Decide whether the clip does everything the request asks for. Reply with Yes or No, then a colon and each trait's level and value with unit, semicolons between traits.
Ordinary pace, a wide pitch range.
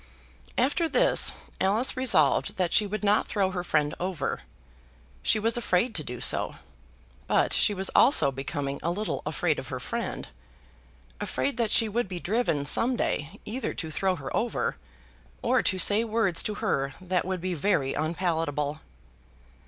Yes: average, 160 wpm; wide, 5.9 semitones